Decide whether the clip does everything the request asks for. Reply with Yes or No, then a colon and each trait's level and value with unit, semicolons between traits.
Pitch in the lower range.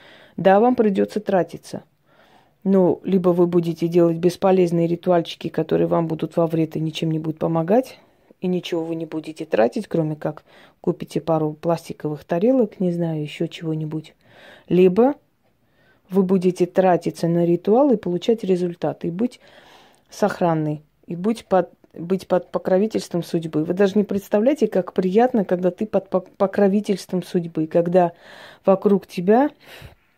No: medium, 180 Hz